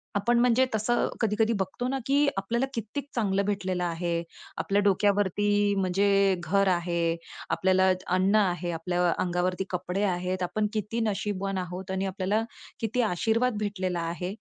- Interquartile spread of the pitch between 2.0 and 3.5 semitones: Yes, average, 2.8 semitones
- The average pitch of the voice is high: Yes, high, 195 Hz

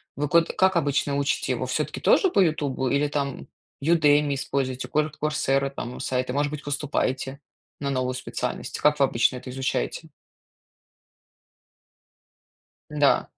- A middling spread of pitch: No, narrow, 2.2 semitones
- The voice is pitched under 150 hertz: Yes, medium, 140 Hz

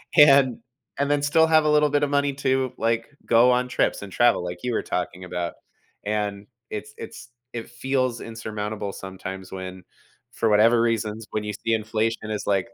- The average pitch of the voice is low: Yes, low, 115 Hz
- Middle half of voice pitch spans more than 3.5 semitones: Yes, average, 4.0 semitones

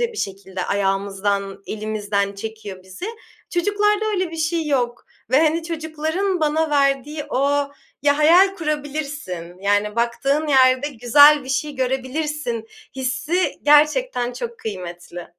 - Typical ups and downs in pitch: No, wide, 6.6 semitones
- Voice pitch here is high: Yes, very high, 275 Hz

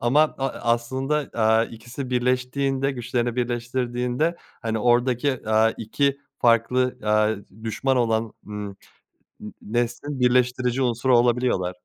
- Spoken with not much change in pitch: Yes, narrow, 2.2 semitones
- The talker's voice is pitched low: Yes, low, 120 Hz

